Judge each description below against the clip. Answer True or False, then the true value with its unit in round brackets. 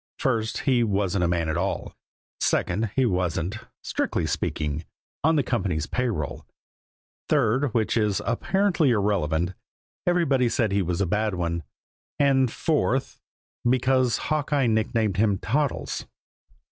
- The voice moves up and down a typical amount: False (6.5 semitones)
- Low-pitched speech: True (110 Hz)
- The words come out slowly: True (130 wpm)